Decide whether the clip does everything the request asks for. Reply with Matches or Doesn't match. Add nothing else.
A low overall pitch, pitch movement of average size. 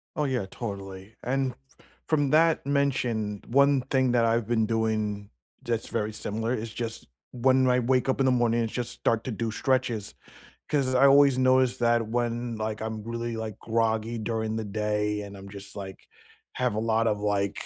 Matches